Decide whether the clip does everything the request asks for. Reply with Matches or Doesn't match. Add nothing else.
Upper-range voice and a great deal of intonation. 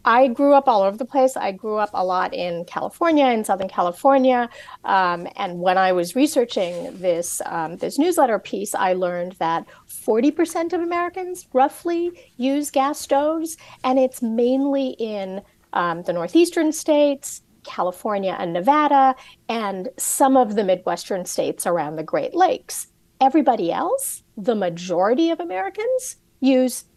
Matches